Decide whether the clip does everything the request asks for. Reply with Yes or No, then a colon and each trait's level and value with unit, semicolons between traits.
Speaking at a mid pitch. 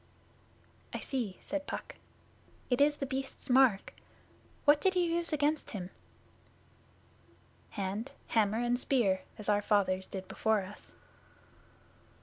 No: high, 240 Hz